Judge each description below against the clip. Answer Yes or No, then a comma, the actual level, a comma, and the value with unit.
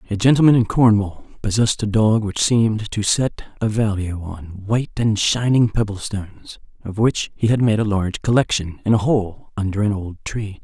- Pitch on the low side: Yes, low, 105 Hz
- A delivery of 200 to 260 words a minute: No, average, 190 wpm